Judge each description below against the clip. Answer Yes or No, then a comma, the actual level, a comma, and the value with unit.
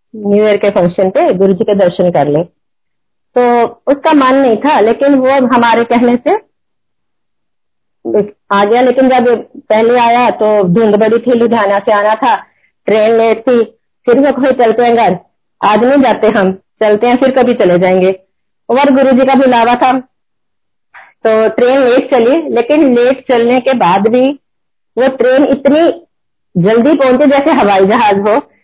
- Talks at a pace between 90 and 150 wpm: No, average, 165 wpm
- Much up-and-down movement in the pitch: No, average, 3.8 semitones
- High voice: Yes, high, 235 Hz